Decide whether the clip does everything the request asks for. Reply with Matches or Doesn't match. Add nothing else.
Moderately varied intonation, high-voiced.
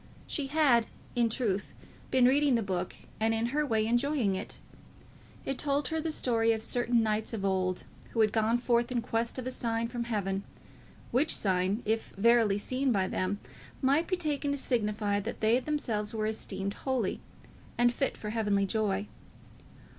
Matches